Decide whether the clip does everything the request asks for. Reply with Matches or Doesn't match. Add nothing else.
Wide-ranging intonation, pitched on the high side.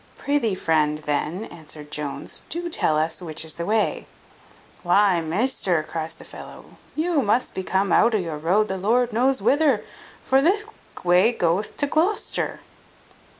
Matches